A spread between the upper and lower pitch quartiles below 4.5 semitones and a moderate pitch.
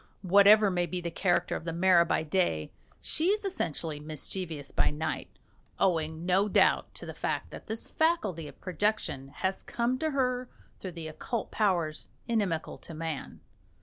No: average, 5.1 semitones; medium, 180 Hz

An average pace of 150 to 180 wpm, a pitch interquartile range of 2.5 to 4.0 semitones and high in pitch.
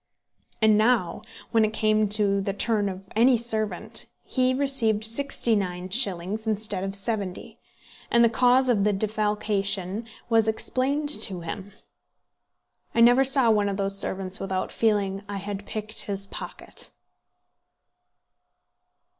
No: average, 140 wpm; average, 2.8 semitones; high, 215 Hz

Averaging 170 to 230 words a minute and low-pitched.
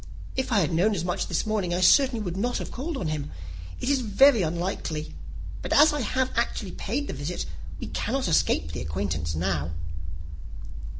No: average, 185 wpm; medium, 180 Hz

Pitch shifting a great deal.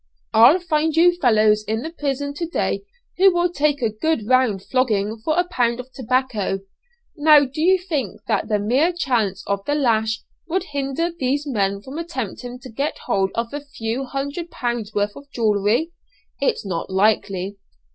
Yes: wide, 5.9 semitones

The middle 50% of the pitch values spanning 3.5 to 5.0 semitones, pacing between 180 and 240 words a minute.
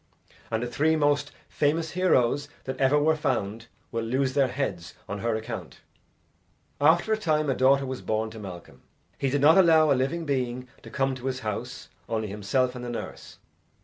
Yes: average, 4.1 semitones; average, 185 wpm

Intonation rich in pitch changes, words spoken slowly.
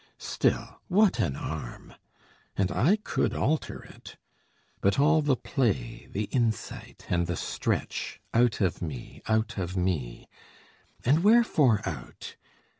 Yes: wide, 8.8 semitones; slow, 125 wpm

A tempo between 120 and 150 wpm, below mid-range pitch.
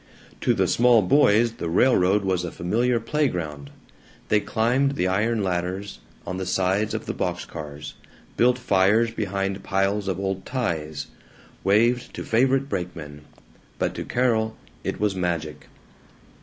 Yes: average, 145 wpm; low, 100 Hz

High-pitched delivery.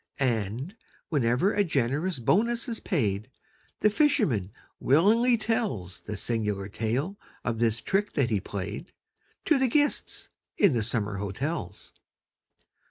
No: low, 130 Hz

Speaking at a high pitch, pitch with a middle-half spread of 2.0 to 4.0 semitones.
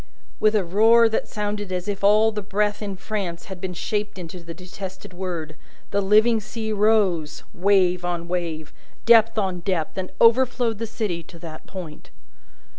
Yes: high, 195 Hz; average, 3.4 semitones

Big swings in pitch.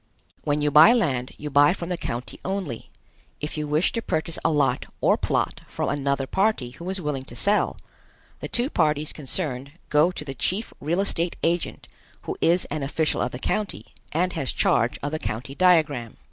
No: average, 4.5 semitones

